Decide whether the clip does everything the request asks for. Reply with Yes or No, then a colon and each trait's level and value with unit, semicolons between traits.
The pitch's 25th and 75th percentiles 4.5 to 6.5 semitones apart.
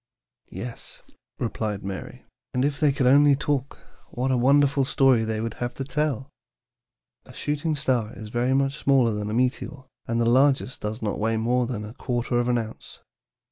No: average, 3.2 semitones